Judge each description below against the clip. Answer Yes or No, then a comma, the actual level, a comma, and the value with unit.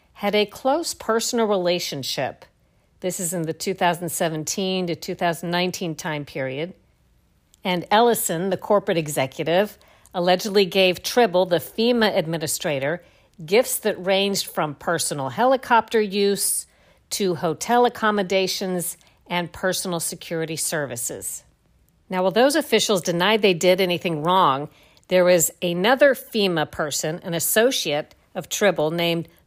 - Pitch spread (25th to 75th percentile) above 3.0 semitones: Yes, average, 3.6 semitones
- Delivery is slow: Yes, slow, 120 wpm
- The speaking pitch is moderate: Yes, medium, 180 Hz